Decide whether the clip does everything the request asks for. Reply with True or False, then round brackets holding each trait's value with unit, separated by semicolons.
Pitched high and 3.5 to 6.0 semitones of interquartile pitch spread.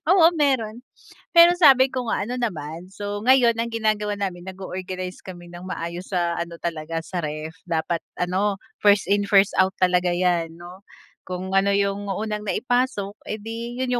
True (195 Hz; 4.0 semitones)